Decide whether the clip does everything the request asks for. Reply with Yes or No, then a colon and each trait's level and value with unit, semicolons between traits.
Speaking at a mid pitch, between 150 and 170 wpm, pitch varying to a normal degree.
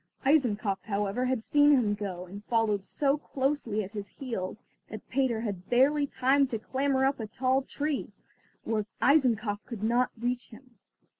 No: high, 240 Hz; average, 160 wpm; average, 4.4 semitones